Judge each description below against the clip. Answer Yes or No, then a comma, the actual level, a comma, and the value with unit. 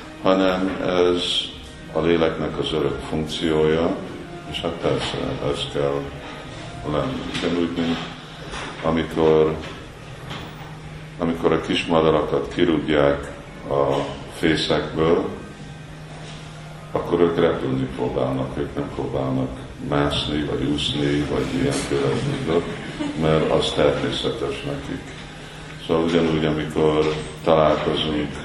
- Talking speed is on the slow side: Yes, slow, 90 wpm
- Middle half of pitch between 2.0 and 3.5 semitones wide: Yes, narrow, 2.4 semitones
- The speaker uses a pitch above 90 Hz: No, very low, 75 Hz